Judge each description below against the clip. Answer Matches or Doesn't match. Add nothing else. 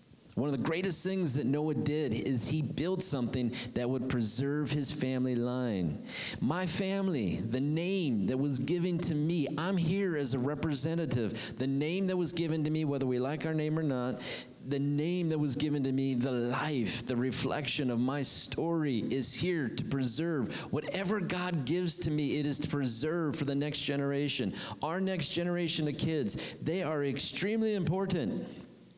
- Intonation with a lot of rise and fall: Doesn't match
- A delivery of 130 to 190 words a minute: Matches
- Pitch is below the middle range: Doesn't match